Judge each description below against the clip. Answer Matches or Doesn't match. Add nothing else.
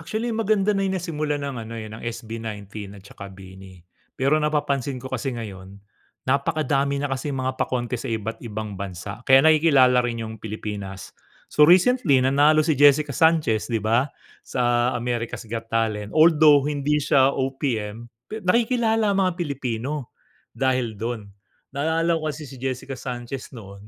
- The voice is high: Doesn't match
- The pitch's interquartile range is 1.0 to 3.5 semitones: Doesn't match